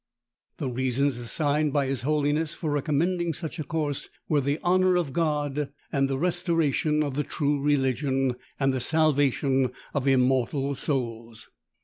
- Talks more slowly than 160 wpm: Yes, average, 140 wpm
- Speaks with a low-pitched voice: No, medium, 145 Hz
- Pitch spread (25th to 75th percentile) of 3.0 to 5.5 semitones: No, narrow, 2.5 semitones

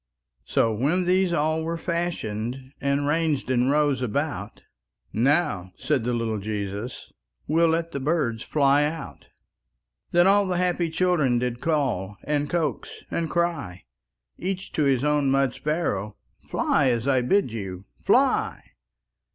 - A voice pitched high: No, medium, 145 Hz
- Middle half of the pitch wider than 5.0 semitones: Yes, wide, 5.6 semitones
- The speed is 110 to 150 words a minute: Yes, average, 140 wpm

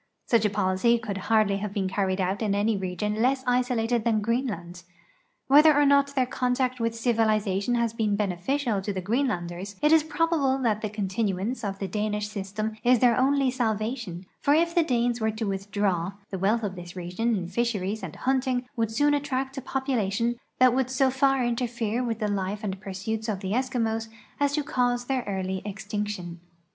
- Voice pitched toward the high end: Yes, high, 220 Hz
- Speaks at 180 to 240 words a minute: Yes, average, 185 wpm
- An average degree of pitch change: Yes, average, 4.2 semitones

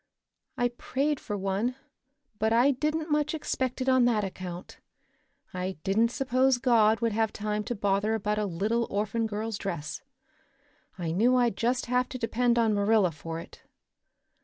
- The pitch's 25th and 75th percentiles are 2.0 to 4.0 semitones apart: Yes, average, 3.6 semitones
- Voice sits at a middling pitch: No, high, 225 Hz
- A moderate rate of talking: Yes, average, 160 wpm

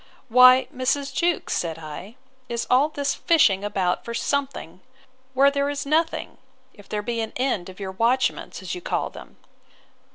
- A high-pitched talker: Yes, very high, 250 Hz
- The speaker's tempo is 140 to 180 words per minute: Yes, average, 165 wpm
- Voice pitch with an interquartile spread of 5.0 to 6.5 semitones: Yes, wide, 5.5 semitones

